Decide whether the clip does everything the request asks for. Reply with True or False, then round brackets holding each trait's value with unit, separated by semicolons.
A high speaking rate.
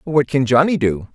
True (210 wpm)